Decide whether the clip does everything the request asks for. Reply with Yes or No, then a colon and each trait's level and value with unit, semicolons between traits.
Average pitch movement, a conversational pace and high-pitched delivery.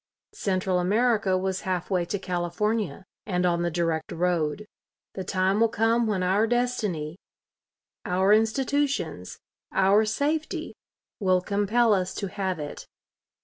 No: average, 3.5 semitones; slow, 130 wpm; high, 195 Hz